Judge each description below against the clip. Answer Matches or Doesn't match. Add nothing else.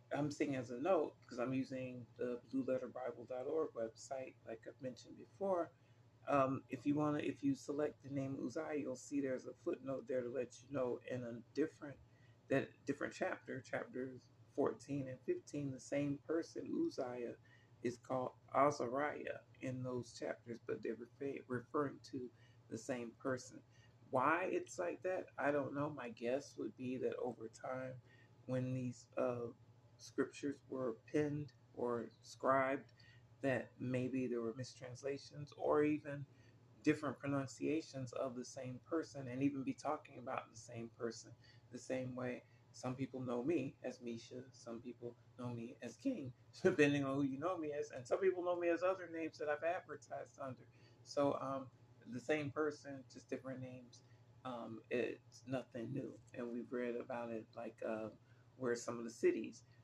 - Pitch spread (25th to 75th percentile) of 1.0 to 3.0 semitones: Matches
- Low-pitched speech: Matches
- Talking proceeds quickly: Doesn't match